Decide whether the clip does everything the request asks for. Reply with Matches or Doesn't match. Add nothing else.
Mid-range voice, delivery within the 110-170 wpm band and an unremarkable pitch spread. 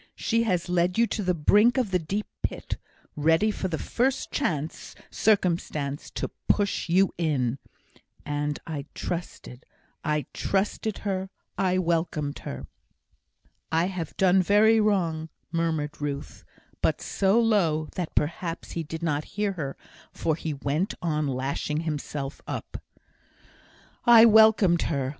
Matches